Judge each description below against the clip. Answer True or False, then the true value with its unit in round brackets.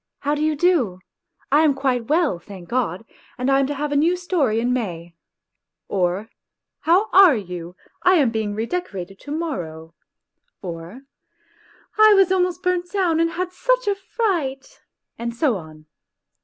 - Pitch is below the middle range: False (275 Hz)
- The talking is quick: False (165 wpm)